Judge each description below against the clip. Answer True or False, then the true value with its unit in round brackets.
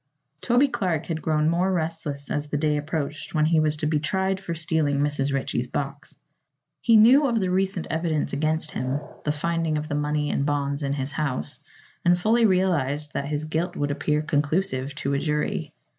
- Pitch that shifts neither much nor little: True (3.0 semitones)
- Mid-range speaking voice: True (155 Hz)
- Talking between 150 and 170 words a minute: False (190 wpm)